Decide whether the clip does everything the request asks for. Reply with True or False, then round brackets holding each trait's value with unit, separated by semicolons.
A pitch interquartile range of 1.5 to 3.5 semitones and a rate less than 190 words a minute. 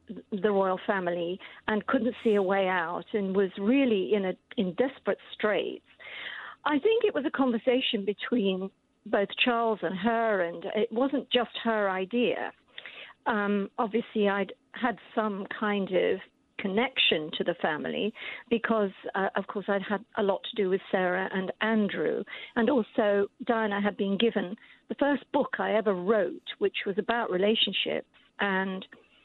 True (3.2 semitones; 155 wpm)